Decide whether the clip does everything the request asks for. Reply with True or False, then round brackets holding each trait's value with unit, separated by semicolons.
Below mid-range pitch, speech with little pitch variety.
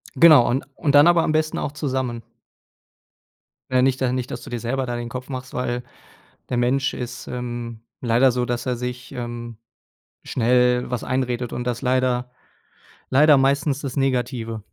True (125 Hz; 1.6 semitones)